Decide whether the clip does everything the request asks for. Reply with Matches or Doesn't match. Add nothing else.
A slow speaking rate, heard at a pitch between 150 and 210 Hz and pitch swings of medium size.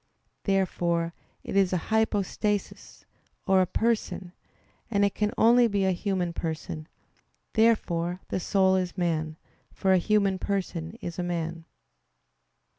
Matches